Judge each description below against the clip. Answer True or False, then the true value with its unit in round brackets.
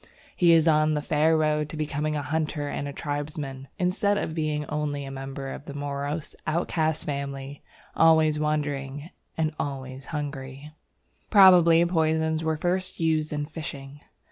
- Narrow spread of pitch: True (1.9 semitones)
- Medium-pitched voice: True (150 Hz)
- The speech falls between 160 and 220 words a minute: False (145 wpm)